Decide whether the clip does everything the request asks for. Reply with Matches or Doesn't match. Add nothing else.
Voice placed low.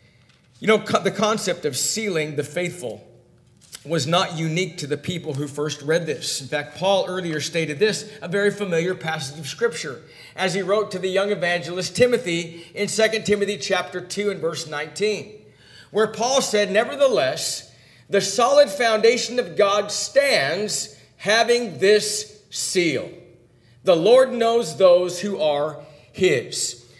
Doesn't match